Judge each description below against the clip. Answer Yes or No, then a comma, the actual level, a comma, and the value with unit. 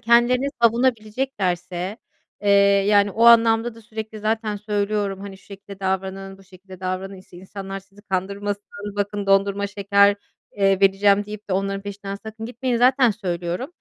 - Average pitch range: No, narrow, 2.1 semitones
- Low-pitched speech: No, high, 200 Hz